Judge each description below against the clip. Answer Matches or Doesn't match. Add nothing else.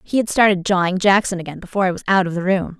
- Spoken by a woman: Matches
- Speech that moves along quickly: Matches